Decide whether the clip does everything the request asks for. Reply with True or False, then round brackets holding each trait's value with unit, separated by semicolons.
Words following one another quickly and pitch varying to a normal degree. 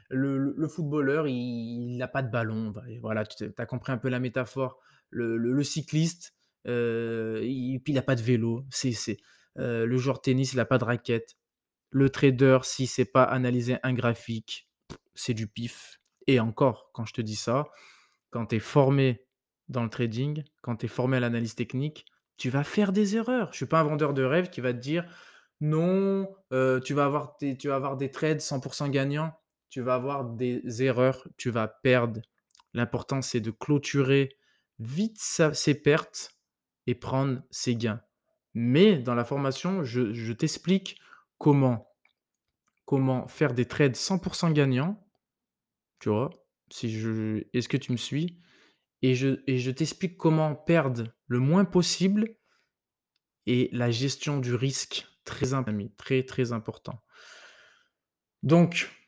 False (165 wpm; 3.7 semitones)